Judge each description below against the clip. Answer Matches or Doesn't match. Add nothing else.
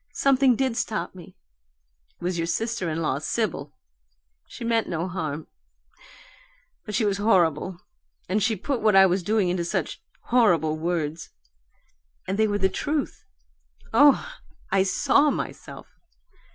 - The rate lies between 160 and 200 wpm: Doesn't match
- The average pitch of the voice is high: Matches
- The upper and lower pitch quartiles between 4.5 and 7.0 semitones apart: Matches